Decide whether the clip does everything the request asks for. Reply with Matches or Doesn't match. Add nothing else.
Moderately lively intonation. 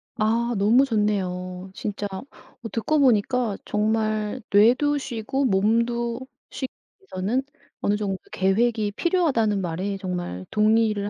Matches